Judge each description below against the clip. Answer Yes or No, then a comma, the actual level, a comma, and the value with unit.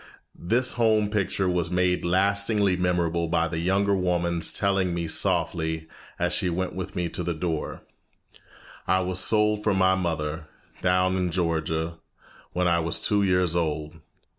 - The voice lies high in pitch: No, very low, 90 Hz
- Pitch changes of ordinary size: No, narrow, 2.2 semitones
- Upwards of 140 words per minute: Yes, average, 155 wpm